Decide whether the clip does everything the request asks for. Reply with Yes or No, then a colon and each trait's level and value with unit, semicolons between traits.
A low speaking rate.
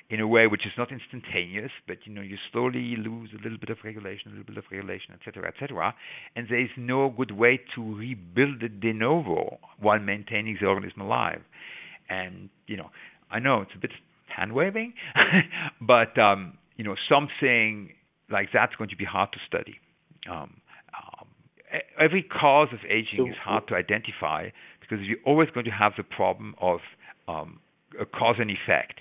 No: average, 185 wpm